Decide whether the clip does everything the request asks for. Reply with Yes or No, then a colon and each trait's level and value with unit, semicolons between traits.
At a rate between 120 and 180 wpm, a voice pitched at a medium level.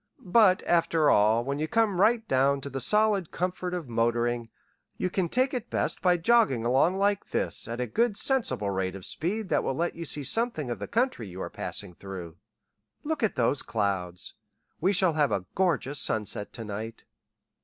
No: average, 190 wpm; medium, 150 Hz